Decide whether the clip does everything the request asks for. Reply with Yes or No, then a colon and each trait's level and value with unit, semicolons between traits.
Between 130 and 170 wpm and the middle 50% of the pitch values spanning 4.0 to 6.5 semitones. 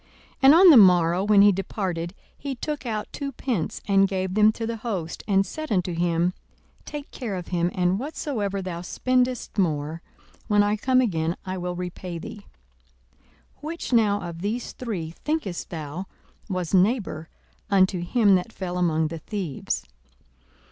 Yes: average, 165 wpm; average, 4.6 semitones